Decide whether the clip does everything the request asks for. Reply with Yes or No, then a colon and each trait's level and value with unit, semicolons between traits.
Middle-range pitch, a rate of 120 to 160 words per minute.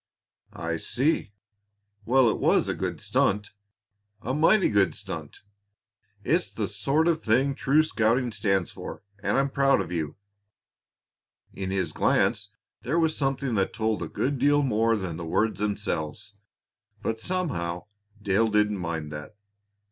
No: low, 110 Hz; average, 145 wpm